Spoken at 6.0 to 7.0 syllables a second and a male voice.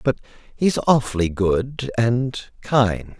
No: 3.0 syllables/s; male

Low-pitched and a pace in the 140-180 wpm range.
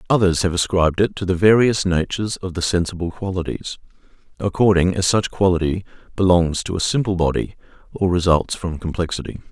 Yes: very low, 90 Hz; average, 160 wpm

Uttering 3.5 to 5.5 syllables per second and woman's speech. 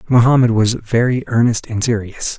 No: 5.1 syllables/s; male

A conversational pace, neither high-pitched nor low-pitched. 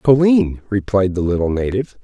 No: average, 145 wpm; low, 105 Hz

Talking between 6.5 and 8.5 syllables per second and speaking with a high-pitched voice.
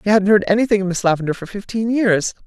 Yes: 6.6 syllables/s; high, 200 Hz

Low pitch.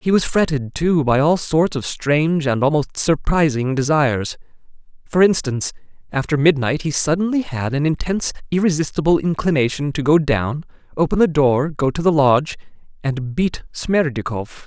No: medium, 150 Hz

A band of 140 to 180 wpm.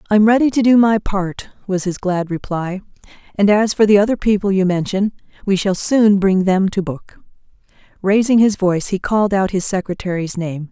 No: average, 195 wpm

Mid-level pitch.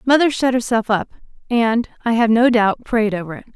No: high, 230 Hz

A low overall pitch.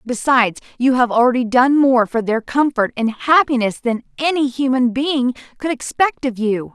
No: very high, 255 Hz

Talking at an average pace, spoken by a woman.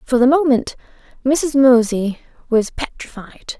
No: slow, 115 wpm; female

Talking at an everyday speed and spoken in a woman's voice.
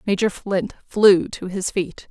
Yes: average, 170 wpm; female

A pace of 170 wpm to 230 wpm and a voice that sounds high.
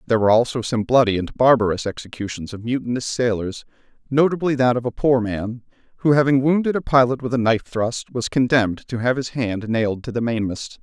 No: average, 200 wpm; low, 120 Hz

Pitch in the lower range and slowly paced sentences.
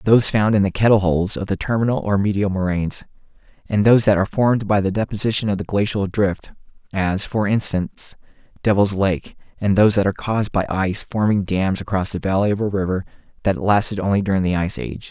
No: low, 100 Hz; fast, 205 wpm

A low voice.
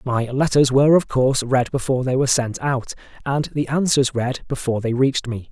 Yes: low, 130 Hz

